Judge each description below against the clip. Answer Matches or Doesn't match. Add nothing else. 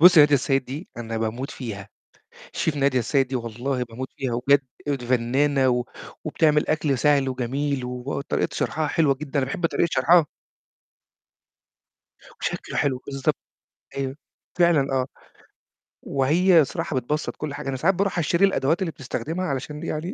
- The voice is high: Doesn't match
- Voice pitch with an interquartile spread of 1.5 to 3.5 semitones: Matches